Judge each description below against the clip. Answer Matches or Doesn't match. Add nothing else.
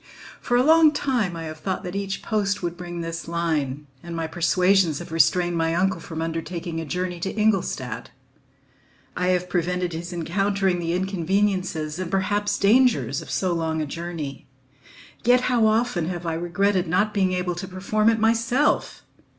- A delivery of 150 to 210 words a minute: Matches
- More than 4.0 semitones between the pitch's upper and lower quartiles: Doesn't match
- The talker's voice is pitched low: Doesn't match